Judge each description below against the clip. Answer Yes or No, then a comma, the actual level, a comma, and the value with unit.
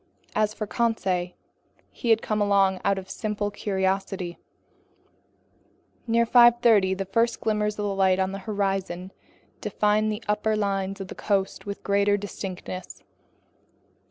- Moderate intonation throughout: No, narrow, 1.8 semitones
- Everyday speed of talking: No, slow, 130 wpm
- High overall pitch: Yes, high, 200 Hz